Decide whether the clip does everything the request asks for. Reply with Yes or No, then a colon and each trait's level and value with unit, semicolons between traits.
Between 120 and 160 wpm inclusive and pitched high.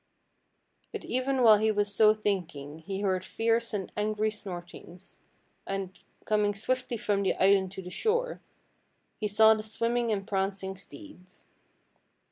Yes: average, 140 wpm; high, 205 Hz